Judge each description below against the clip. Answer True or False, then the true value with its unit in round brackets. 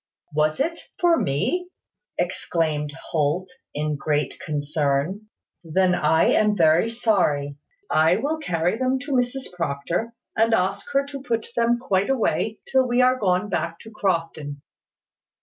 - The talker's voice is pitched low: False (185 Hz)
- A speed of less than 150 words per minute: True (140 wpm)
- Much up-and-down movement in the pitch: True (7.4 semitones)